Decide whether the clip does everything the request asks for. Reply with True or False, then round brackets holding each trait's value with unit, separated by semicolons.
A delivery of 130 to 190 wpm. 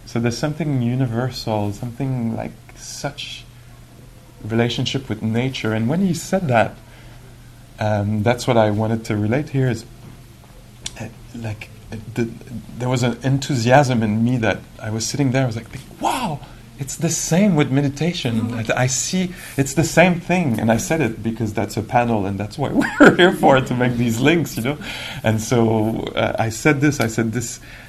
True (185 wpm)